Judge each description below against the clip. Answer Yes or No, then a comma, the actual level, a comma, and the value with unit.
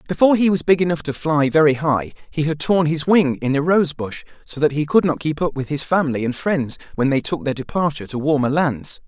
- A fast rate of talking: Yes, fast, 245 wpm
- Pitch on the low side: No, medium, 150 Hz